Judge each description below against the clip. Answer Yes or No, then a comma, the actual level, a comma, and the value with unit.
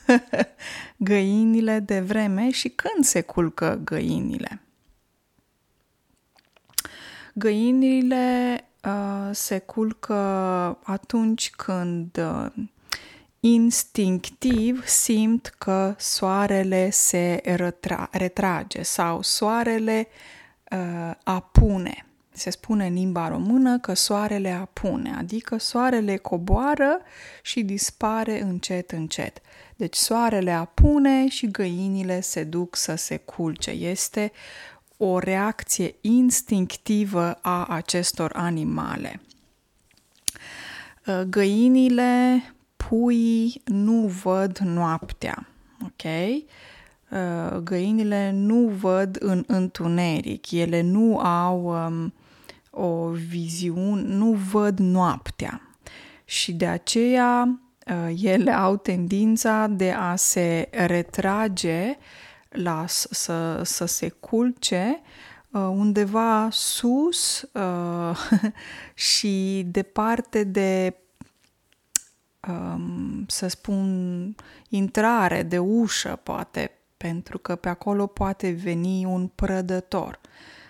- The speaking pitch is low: No, high, 195 Hz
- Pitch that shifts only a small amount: No, average, 4.0 semitones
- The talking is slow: Yes, slow, 85 wpm